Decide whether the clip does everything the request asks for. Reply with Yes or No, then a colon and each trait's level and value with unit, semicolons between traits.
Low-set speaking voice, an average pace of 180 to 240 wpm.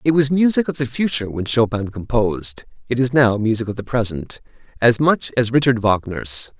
Yes: low, 120 Hz; average, 190 wpm